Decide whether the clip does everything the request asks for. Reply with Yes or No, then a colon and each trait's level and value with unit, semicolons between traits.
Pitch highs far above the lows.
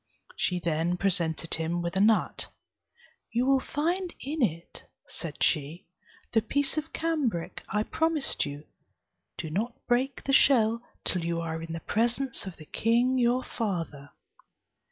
Yes: wide, 7.7 semitones